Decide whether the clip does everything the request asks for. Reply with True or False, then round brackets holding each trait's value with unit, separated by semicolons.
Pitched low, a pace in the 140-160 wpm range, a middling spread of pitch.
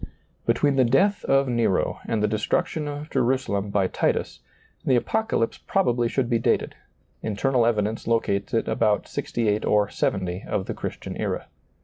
True (115 Hz; 150 wpm; 4.2 semitones)